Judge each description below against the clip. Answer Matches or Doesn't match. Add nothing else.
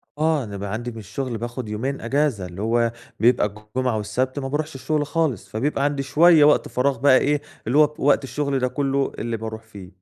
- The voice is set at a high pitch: Doesn't match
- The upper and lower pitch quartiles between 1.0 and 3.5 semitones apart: Doesn't match